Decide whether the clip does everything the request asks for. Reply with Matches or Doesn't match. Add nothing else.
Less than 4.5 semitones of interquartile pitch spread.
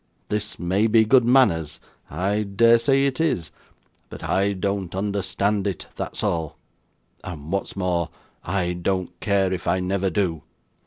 Matches